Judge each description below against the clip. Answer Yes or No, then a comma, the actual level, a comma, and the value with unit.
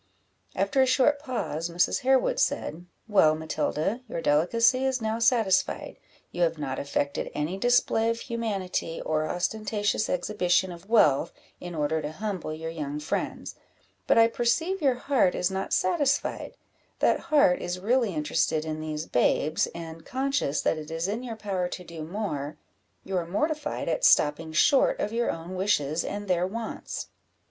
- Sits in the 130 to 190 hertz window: Yes, medium, 185 Hz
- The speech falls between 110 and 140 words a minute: No, average, 160 wpm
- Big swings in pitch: Yes, wide, 6.5 semitones